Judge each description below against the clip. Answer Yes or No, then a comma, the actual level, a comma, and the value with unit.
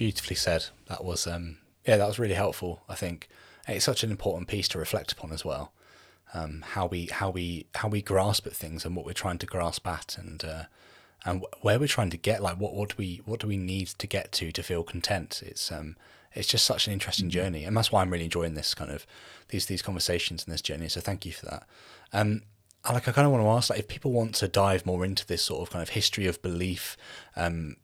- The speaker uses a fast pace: Yes, fast, 250 wpm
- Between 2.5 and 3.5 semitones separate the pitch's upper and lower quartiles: Yes, average, 3.2 semitones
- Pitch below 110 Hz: Yes, very low, 95 Hz